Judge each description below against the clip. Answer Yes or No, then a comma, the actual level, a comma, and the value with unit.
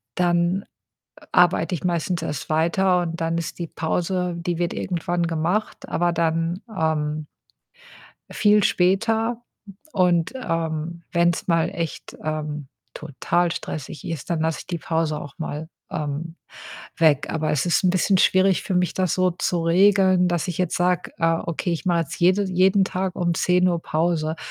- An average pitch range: No, narrow, 2.0 semitones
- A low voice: No, medium, 170 Hz